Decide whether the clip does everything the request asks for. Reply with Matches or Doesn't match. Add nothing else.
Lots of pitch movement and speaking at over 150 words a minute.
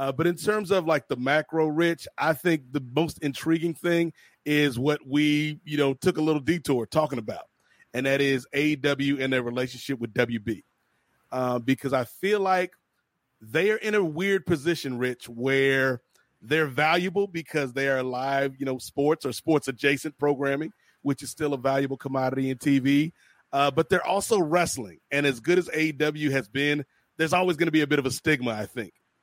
Doesn't match